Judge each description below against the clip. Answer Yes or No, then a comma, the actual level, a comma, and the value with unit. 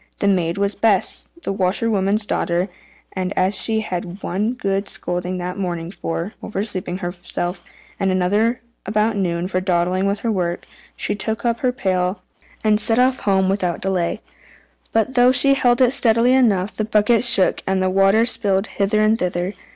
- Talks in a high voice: Yes, high, 195 Hz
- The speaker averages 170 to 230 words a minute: Yes, average, 175 wpm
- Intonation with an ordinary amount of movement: Yes, average, 3.2 semitones